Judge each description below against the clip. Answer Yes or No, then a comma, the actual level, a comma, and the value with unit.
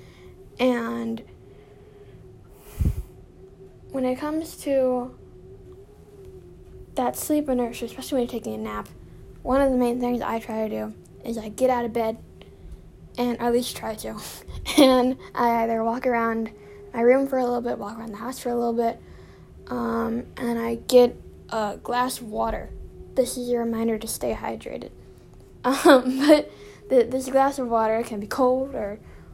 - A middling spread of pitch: No, narrow, 2.2 semitones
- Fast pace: No, average, 165 wpm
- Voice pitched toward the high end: Yes, high, 240 Hz